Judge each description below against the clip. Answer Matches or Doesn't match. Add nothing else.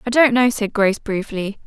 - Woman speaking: Matches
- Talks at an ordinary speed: Doesn't match